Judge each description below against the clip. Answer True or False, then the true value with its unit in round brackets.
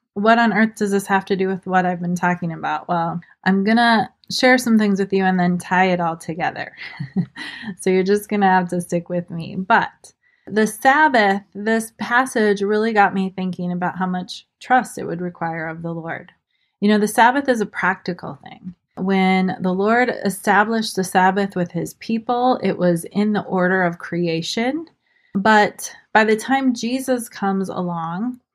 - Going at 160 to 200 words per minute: True (185 wpm)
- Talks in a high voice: True (195 Hz)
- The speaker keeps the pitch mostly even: False (3.8 semitones)